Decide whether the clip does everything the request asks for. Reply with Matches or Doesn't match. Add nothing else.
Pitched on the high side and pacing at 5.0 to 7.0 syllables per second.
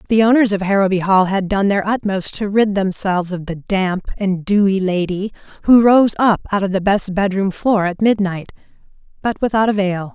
Matches